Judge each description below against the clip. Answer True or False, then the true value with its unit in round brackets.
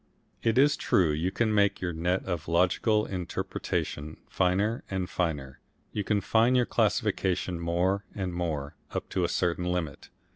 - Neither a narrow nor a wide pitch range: True (3.1 semitones)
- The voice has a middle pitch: False (90 Hz)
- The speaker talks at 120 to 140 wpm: False (155 wpm)